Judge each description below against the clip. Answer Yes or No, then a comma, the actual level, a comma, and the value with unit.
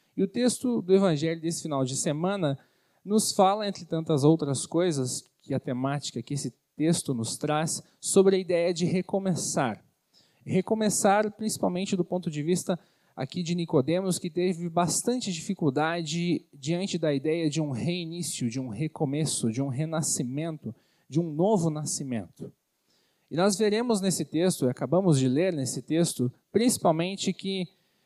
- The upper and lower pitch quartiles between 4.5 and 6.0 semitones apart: No, average, 4.0 semitones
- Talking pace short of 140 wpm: No, average, 150 wpm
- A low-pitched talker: No, medium, 170 Hz